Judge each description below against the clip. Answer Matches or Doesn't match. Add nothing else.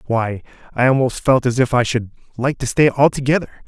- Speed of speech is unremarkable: Matches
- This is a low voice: Matches